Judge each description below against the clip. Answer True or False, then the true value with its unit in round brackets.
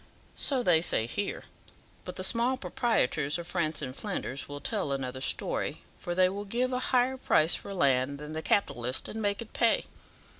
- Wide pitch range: True (8.4 semitones)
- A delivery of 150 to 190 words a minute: True (185 wpm)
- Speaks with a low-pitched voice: False (180 Hz)